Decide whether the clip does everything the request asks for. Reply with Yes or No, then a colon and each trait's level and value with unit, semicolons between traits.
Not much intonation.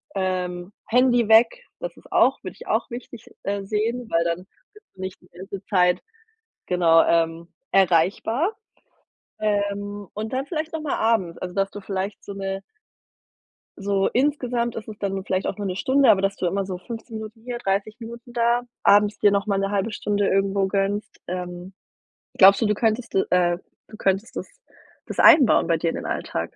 No: average, 3.3 semitones